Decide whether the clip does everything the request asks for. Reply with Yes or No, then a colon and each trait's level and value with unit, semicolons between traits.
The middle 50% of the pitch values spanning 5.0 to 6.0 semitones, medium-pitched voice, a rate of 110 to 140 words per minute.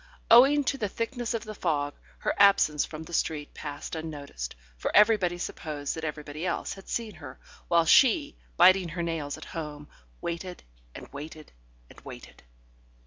No: wide, 5.4 semitones; medium, 170 Hz; average, 160 wpm